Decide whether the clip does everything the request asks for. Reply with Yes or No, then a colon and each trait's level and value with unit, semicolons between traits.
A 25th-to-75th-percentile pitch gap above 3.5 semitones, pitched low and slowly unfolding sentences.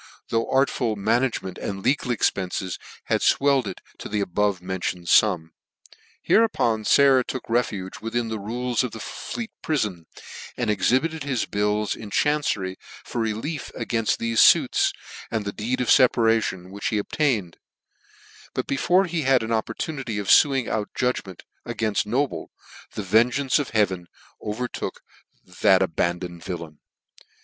No: average, 4.4 semitones; low, 110 Hz; average, 145 wpm